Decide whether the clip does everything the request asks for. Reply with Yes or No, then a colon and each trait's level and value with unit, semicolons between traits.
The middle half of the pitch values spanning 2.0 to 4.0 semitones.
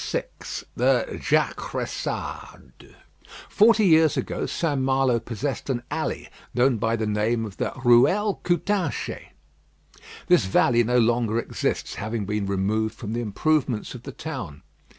No: average, 4.8 semitones